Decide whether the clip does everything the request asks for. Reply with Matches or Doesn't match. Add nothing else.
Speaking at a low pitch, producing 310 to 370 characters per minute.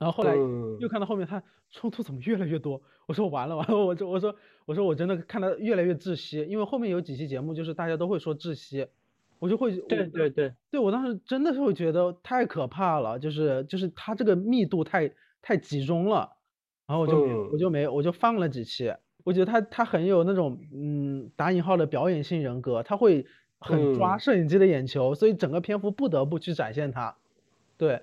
Doesn't match